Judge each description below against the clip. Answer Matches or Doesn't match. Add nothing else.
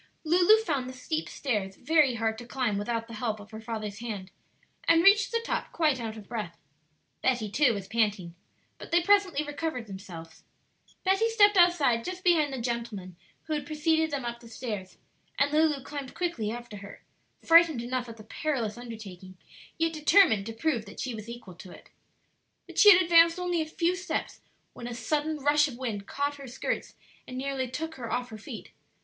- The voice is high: Matches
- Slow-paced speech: Doesn't match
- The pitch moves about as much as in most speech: Doesn't match